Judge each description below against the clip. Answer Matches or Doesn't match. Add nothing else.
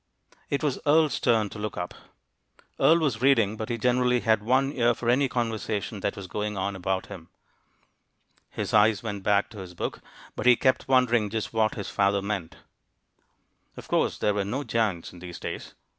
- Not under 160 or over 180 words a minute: Doesn't match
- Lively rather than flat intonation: Doesn't match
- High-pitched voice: Doesn't match